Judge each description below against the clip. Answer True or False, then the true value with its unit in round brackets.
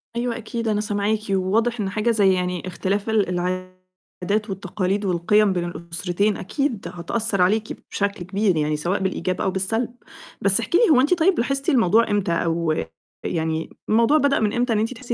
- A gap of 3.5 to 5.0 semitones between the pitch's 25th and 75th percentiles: True (3.8 semitones)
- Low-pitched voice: False (200 Hz)